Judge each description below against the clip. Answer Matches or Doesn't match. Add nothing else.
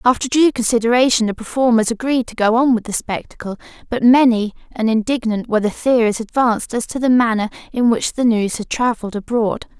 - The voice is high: Matches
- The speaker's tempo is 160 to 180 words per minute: Doesn't match